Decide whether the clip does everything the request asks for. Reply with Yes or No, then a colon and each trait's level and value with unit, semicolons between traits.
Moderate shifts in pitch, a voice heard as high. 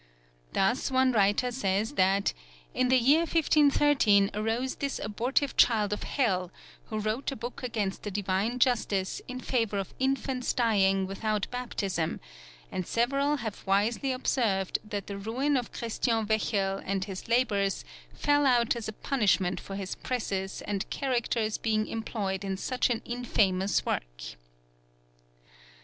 Yes: average, 4.2 semitones; high, 220 Hz